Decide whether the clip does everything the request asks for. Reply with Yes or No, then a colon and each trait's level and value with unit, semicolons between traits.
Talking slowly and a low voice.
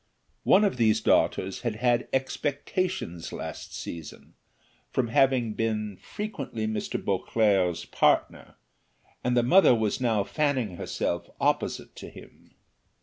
Yes: slow, 120 wpm; low, 115 Hz